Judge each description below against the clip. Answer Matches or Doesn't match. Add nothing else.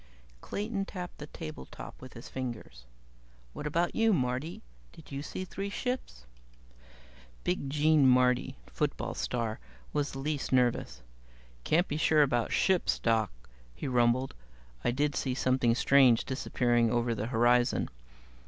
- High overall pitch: Doesn't match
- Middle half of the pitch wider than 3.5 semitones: Matches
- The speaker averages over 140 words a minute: Doesn't match